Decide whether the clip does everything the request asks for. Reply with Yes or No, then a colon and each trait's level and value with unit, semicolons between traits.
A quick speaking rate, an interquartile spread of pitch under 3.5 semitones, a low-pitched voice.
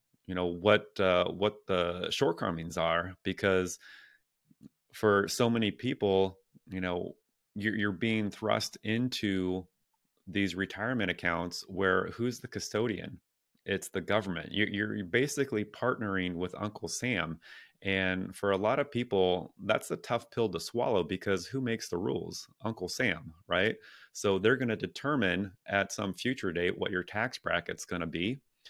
No: average, 155 wpm; average, 2.9 semitones; low, 100 Hz